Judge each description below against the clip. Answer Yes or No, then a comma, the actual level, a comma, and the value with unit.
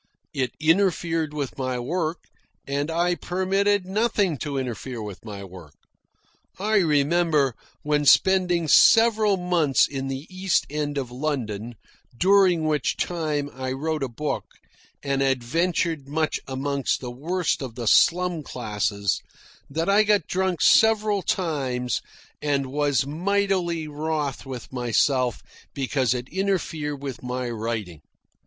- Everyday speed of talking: No, slow, 130 wpm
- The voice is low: No, medium, 150 Hz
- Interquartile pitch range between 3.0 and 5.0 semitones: No, wide, 5.4 semitones